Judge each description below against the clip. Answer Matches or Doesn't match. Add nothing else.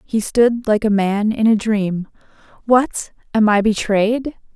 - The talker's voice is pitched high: Matches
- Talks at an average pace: Matches